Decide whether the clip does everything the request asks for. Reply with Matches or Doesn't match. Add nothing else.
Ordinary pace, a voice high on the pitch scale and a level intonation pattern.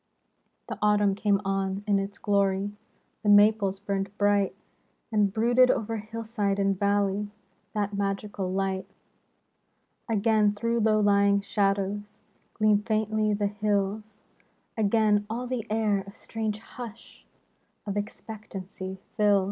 Doesn't match